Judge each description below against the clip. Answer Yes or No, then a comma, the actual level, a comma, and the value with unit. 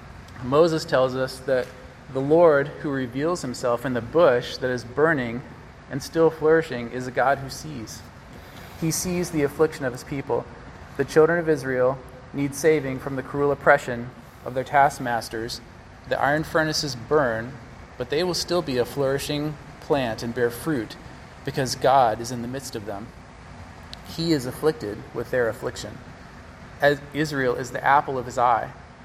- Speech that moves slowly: No, average, 165 wpm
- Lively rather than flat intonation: No, average, 3.6 semitones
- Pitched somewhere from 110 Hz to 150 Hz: Yes, low, 135 Hz